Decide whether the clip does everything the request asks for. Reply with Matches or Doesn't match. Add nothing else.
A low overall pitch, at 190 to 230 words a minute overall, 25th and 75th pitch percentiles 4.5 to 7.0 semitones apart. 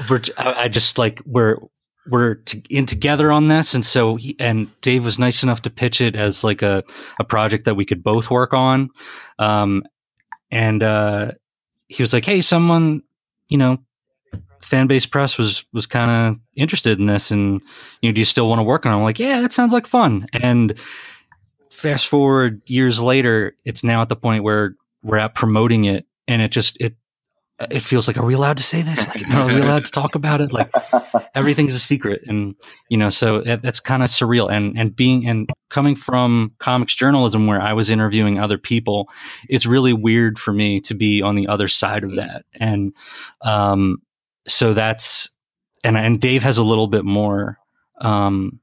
Doesn't match